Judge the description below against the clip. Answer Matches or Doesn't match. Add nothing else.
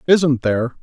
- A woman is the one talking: Doesn't match